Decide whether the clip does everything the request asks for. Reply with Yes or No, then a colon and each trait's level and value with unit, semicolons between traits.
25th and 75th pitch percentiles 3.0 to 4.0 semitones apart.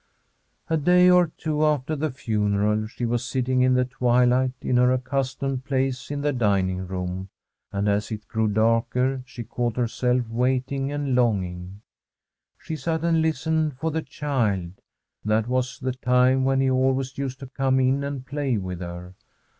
Yes: average, 3.7 semitones